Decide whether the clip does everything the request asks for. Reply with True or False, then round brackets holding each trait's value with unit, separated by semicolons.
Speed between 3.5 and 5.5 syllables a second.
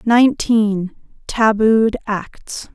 False (2.8 syllables/s)